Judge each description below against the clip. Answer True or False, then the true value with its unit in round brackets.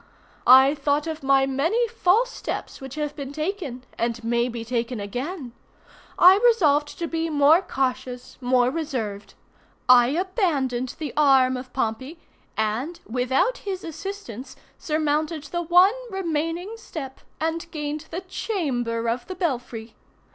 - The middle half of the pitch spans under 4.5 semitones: False (5.2 semitones)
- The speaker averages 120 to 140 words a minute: True (135 wpm)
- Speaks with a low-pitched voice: False (290 Hz)